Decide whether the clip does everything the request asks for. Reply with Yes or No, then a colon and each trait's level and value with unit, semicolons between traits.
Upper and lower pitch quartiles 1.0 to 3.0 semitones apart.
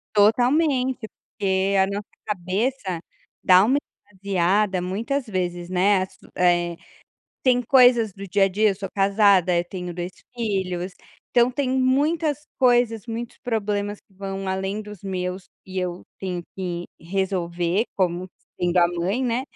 No: average, 4.1 semitones